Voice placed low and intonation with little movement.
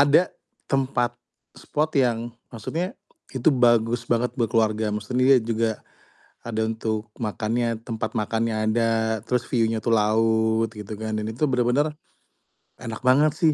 Yes: low, 115 Hz; narrow, 2.0 semitones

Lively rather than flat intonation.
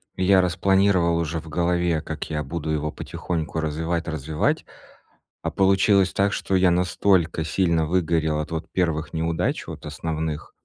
No: narrow, 2.5 semitones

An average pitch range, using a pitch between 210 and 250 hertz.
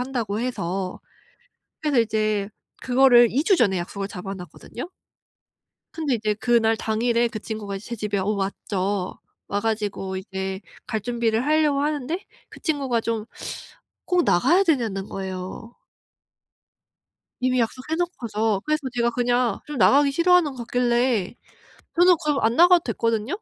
Yes: average, 4.7 semitones; high, 230 Hz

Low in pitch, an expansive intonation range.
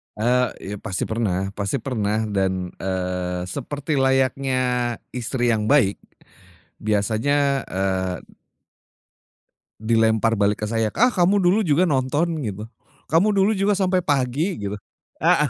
Yes: low, 120 Hz; wide, 5.8 semitones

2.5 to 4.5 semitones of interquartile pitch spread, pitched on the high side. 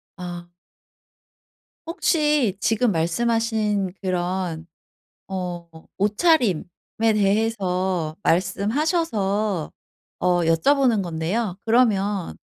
Yes: average, 4.2 semitones; high, 200 Hz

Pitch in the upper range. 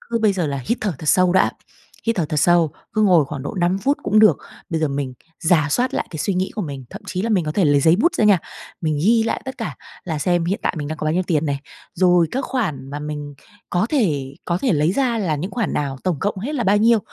No: medium, 175 Hz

